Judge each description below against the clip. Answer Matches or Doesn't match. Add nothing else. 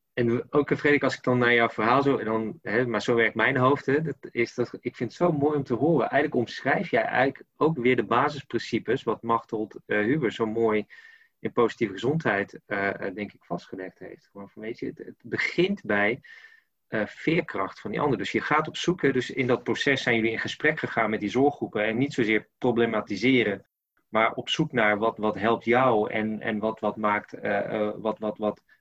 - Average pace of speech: Doesn't match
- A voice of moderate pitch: Doesn't match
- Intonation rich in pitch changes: Doesn't match